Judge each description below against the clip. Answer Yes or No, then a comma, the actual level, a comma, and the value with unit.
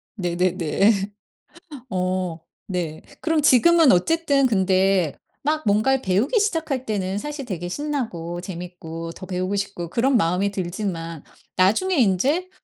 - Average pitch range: No, wide, 7.1 semitones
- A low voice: No, high, 195 Hz